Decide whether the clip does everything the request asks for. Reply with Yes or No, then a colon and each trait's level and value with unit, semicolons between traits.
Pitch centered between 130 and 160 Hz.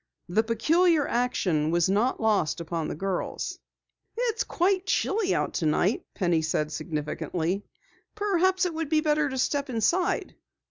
No: high, 230 Hz